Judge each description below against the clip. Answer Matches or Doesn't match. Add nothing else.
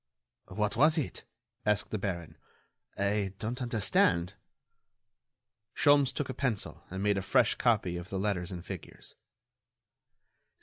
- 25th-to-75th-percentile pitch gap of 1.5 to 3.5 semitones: Doesn't match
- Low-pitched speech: Matches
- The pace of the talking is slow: Matches